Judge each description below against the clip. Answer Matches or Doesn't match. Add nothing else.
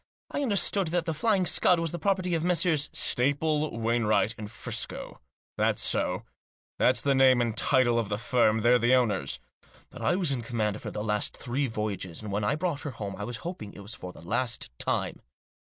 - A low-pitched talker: Matches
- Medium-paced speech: Doesn't match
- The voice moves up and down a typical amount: Doesn't match